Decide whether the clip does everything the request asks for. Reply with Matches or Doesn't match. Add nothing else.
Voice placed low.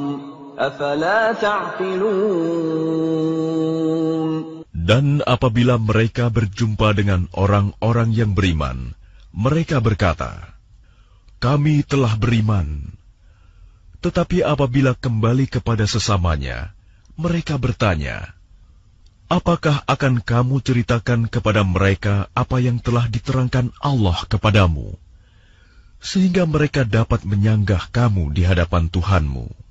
Matches